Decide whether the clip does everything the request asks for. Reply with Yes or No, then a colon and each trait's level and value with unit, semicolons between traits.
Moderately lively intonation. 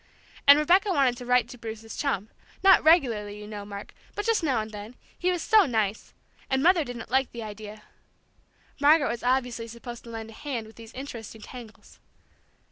Yes: average, 4.5 semitones